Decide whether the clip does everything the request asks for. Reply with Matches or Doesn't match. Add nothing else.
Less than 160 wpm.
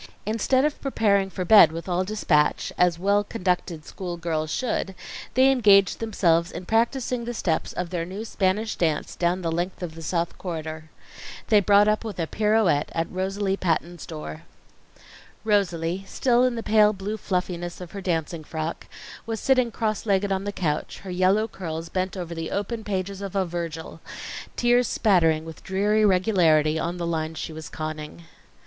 Doesn't match